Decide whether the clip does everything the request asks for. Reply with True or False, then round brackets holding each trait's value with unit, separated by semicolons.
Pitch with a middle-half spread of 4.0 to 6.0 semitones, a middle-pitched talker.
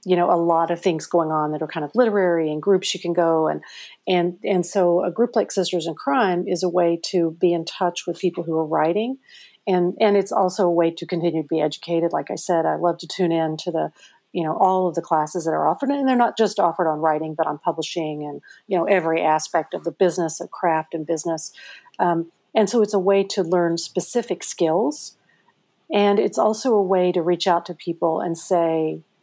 False (2.5 semitones; 175 Hz)